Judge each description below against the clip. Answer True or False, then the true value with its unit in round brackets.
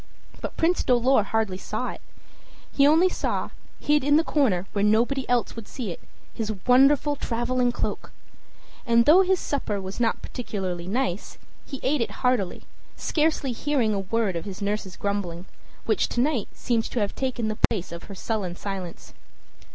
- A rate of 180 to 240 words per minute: False (170 wpm)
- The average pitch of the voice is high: True (230 Hz)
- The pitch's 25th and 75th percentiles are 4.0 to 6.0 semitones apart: True (5.1 semitones)